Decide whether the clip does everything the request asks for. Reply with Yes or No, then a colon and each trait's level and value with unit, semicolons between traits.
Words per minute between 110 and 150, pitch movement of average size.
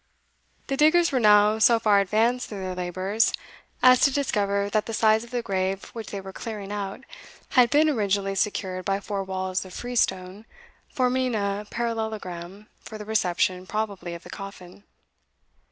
No: average, 165 wpm; average, 3.1 semitones